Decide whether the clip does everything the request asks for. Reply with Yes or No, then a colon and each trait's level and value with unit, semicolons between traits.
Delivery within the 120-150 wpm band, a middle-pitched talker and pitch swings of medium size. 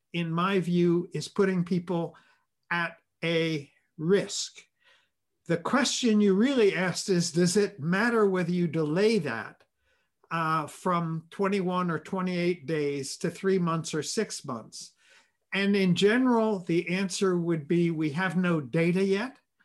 Yes: average, 140 wpm; medium, 180 Hz; average, 3.1 semitones